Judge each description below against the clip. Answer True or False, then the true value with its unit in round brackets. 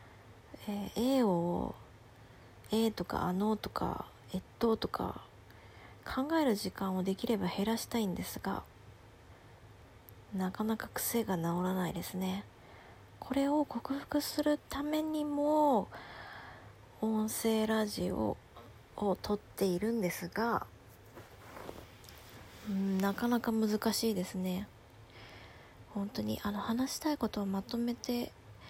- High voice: True (195 Hz)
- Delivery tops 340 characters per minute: False (215 characters per minute)